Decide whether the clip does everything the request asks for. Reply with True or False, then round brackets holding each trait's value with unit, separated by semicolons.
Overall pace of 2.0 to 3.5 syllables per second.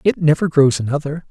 False (5.9 syllables/s)